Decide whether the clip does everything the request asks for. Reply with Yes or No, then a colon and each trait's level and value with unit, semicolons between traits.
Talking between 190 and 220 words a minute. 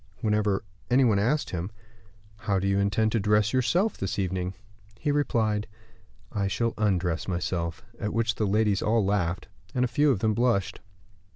No: average, 170 wpm